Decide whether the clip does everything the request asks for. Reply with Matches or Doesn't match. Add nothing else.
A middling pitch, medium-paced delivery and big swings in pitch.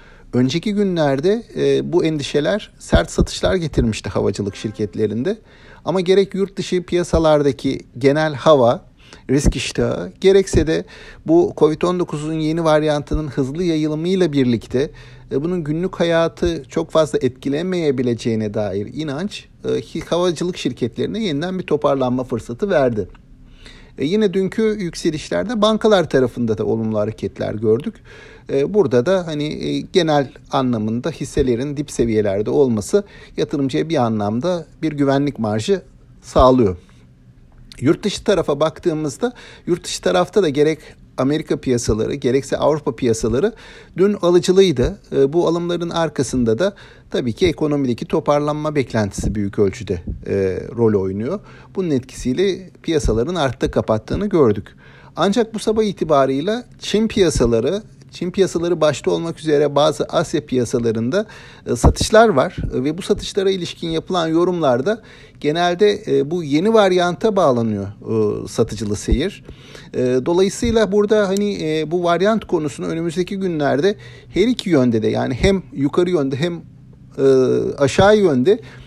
Matches